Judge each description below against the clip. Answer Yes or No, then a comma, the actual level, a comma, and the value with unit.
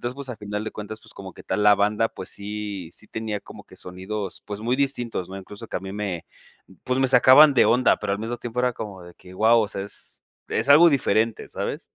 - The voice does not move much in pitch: No, average, 3.3 semitones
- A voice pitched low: Yes, low, 105 Hz